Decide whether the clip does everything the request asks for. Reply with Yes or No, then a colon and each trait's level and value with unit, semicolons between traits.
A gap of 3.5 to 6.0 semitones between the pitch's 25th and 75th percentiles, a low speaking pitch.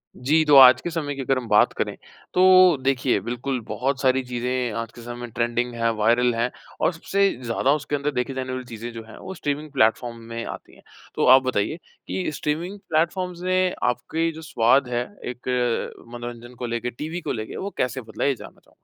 Yes: average, 3.9 semitones; low, 130 Hz